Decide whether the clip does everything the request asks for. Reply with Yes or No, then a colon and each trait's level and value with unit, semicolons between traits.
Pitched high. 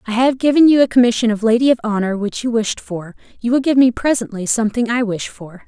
Yes: high, 230 Hz